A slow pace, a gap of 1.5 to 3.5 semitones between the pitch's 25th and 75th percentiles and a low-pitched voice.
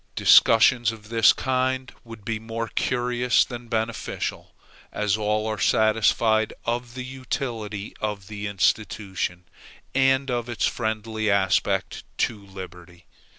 Yes: slow, 120 wpm; narrow, 2.5 semitones; low, 110 Hz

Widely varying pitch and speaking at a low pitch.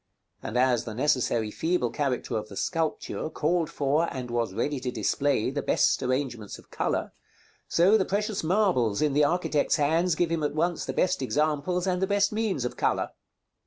No: wide, 5.7 semitones; medium, 150 Hz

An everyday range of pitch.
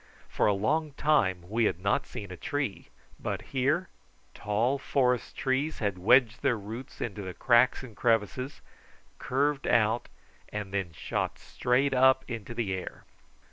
Yes: average, 4.5 semitones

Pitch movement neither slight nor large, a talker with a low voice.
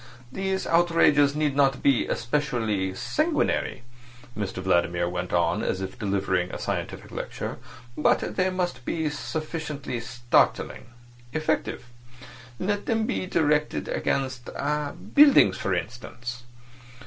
No: wide, 7.1 semitones; low, 130 Hz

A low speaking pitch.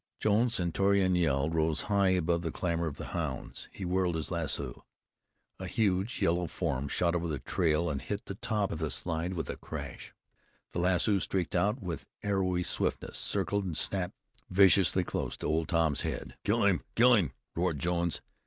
Yes: very low, 90 Hz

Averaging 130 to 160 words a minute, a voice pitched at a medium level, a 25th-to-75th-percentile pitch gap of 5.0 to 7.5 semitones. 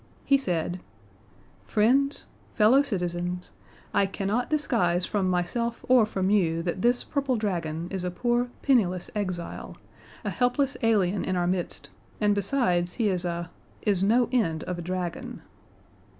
No: average, 145 wpm; high, 195 Hz; average, 5.3 semitones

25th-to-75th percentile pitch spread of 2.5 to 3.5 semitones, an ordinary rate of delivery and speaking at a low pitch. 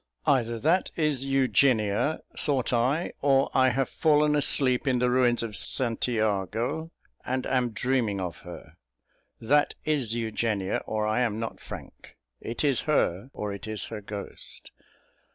No: average, 3.9 semitones; average, 150 wpm; low, 125 Hz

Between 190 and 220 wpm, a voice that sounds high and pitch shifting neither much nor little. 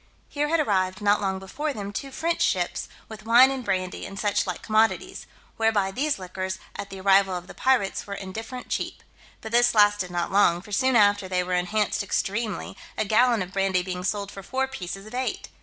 Yes: average, 200 wpm; high, 205 Hz; average, 3.8 semitones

